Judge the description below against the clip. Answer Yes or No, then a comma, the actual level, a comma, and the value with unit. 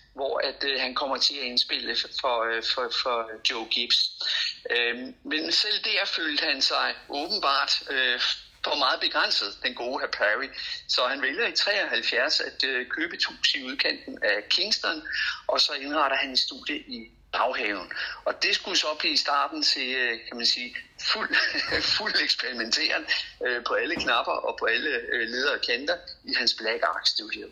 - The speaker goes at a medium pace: Yes, average, 180 wpm